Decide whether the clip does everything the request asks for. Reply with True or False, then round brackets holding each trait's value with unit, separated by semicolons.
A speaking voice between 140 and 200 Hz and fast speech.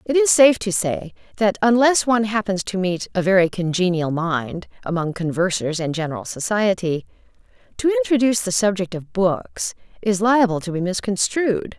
False (190 Hz; 160 wpm)